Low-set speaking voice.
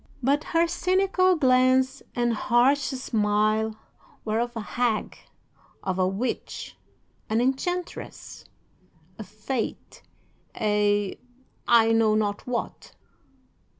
No: high, 240 Hz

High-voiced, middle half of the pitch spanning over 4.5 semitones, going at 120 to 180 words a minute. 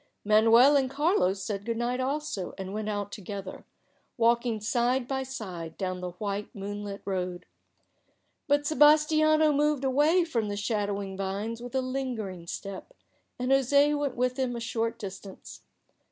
Yes: high, 230 Hz; average, 5.1 semitones; average, 155 wpm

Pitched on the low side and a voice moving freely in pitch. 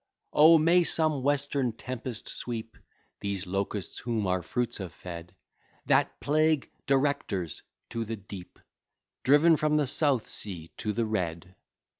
Yes: low, 115 Hz; wide, 6.7 semitones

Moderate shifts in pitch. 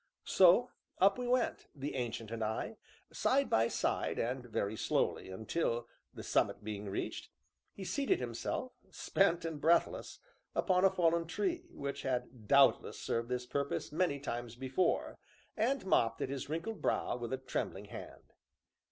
No: wide, 8.1 semitones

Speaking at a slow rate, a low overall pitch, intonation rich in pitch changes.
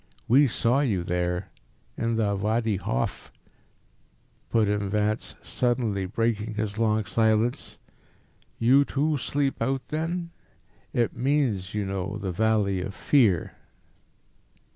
No: slow, 120 wpm; low, 110 Hz; average, 3.9 semitones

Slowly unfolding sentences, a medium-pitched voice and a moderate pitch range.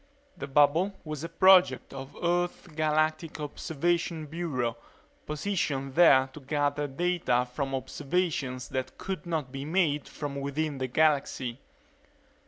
Yes: slow, 125 wpm; medium, 150 Hz; average, 3.7 semitones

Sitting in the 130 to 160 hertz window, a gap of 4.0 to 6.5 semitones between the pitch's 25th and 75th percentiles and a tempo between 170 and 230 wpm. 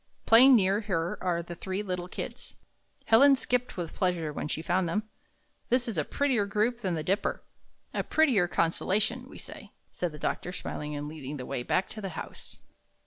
No: medium, 185 Hz; average, 5.2 semitones; average, 190 wpm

